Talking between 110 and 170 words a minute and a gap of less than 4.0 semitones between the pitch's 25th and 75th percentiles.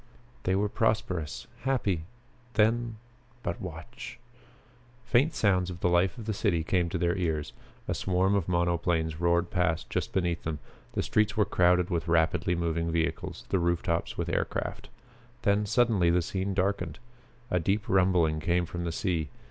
Yes: average, 165 wpm; average, 2.9 semitones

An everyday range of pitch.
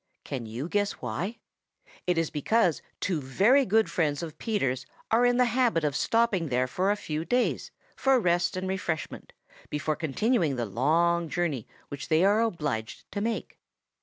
No: wide, 6.9 semitones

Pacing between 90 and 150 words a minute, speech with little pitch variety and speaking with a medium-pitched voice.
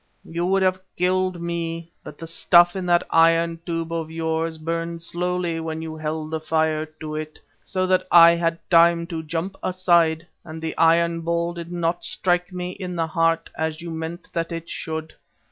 No: average, 185 wpm; narrow, 1.3 semitones; medium, 165 Hz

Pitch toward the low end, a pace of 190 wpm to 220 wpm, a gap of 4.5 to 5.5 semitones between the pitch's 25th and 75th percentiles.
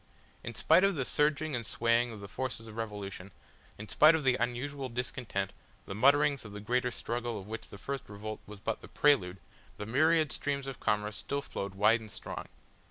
Yes: low, 120 Hz; average, 200 wpm; average, 4.8 semitones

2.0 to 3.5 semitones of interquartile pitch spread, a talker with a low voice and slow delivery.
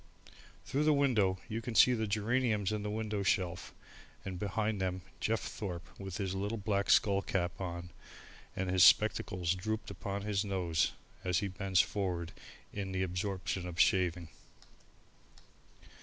No: narrow, 2.6 semitones; low, 100 Hz; average, 150 wpm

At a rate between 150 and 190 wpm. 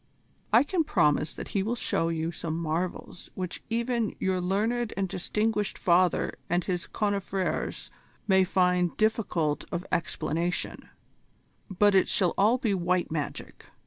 No: average, 140 wpm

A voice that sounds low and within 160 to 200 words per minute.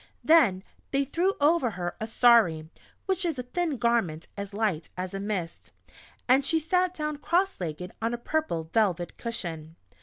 No: high, 230 Hz; average, 170 wpm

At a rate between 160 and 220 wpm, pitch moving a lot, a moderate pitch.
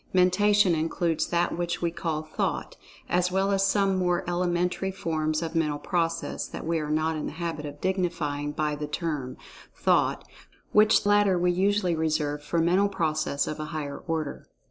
No: average, 170 wpm; average, 2.9 semitones; medium, 170 Hz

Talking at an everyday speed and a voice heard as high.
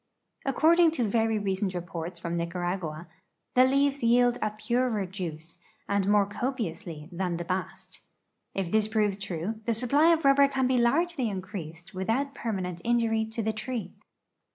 Yes: average, 155 wpm; high, 215 Hz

